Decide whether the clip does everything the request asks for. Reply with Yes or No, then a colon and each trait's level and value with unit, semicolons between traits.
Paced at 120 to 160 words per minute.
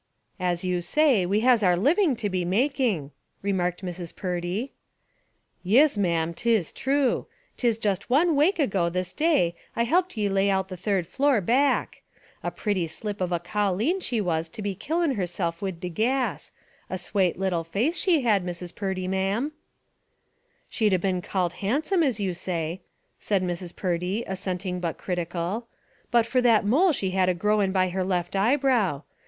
No: average, 170 wpm